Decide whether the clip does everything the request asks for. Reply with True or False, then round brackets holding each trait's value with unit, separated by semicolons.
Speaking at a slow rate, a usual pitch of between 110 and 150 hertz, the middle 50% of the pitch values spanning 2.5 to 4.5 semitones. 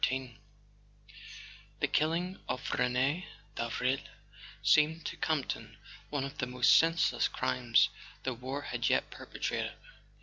True (115 wpm; 135 Hz; 3.8 semitones)